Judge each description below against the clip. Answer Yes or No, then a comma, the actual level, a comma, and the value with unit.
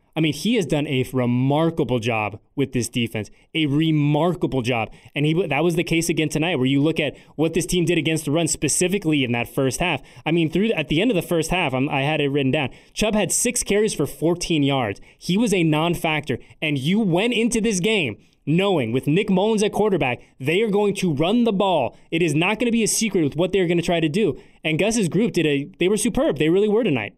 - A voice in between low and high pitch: Yes, medium, 160 Hz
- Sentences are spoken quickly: Yes, fast, 245 wpm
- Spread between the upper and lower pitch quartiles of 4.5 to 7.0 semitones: Yes, average, 5.2 semitones